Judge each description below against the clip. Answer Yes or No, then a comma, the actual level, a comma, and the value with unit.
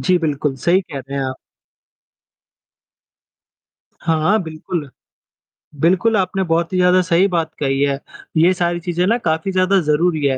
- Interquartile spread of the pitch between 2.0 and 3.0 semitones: No, average, 3.5 semitones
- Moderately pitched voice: Yes, medium, 170 Hz